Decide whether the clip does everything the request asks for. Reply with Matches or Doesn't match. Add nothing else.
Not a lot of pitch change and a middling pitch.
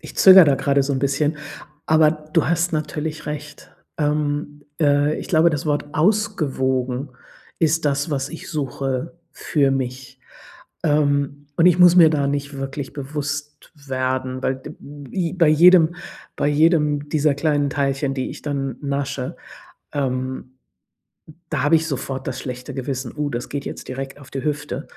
Matches